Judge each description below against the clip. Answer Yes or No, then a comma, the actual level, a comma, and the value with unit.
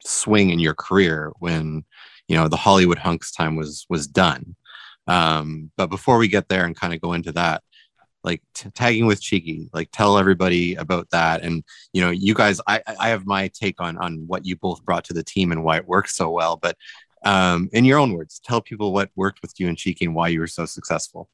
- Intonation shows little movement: No, average, 3.1 semitones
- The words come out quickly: Yes, fast, 230 wpm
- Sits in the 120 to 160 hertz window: No, very low, 90 Hz